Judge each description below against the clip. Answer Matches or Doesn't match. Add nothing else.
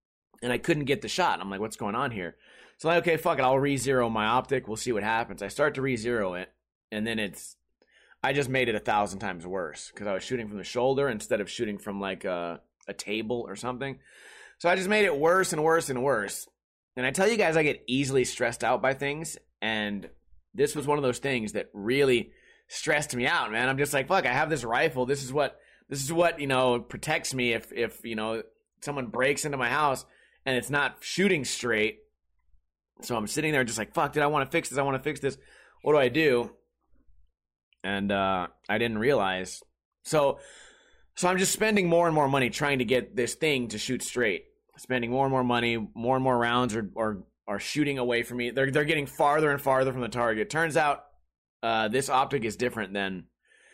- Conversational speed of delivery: Doesn't match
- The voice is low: Matches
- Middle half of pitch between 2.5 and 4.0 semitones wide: Doesn't match